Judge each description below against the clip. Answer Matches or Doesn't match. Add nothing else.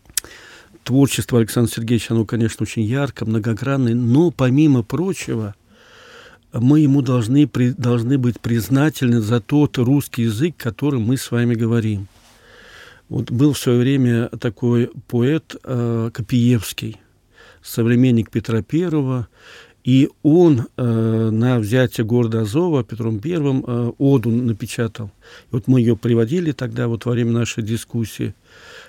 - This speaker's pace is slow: Doesn't match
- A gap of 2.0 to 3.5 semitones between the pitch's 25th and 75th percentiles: Matches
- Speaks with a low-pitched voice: Matches